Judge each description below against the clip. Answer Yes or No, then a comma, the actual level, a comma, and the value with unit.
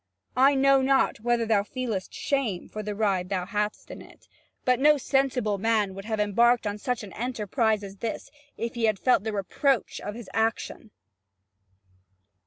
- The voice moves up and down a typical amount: Yes, average, 3.3 semitones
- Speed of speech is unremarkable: Yes, average, 175 wpm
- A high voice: Yes, high, 220 Hz